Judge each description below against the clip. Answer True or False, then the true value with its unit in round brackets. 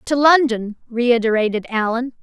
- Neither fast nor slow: False (110 wpm)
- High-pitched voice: True (240 Hz)